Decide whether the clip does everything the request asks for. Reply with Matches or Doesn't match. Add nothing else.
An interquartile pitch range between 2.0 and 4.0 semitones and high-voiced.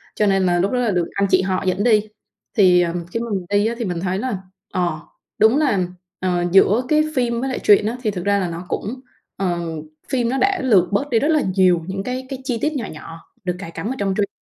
Doesn't match